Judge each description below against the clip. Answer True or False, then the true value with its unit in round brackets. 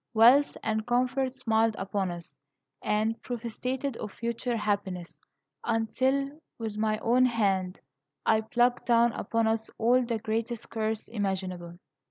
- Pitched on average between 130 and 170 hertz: False (225 Hz)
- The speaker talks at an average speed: False (130 wpm)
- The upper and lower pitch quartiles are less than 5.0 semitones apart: True (2.4 semitones)